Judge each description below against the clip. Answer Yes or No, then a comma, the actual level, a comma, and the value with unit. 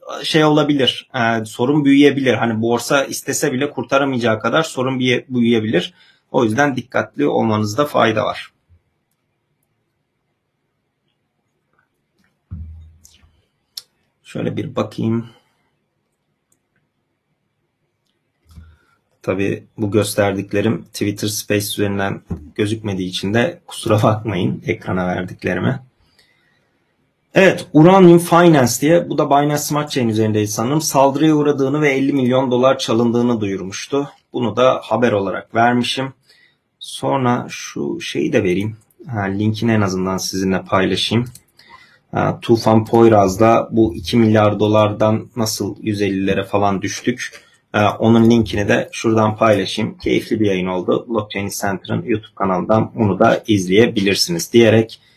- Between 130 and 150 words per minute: No, average, 105 wpm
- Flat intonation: No, average, 4.1 semitones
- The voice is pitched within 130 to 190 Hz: No, low, 110 Hz